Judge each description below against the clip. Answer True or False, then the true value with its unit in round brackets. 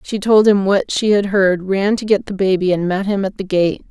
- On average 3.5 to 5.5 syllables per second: True (5.0 syllables/s)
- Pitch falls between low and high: False (195 Hz)